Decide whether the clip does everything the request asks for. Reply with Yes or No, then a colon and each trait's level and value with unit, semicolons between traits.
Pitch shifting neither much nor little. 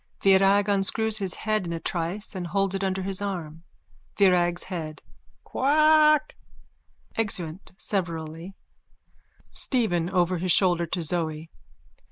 Yes: average, 3.0 semitones